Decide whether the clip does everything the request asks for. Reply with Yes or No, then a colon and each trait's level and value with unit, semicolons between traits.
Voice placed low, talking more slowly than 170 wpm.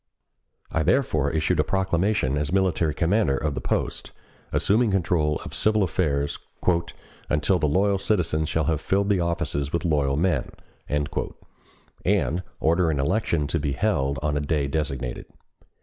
Yes: very low, 80 Hz; average, 150 wpm